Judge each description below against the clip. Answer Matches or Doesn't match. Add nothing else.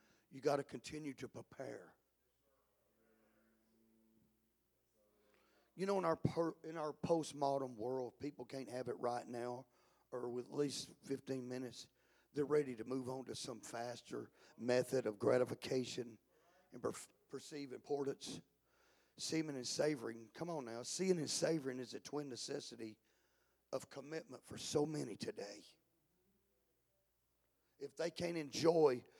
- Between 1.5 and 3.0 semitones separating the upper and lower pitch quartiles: Doesn't match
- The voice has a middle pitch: Doesn't match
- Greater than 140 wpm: Doesn't match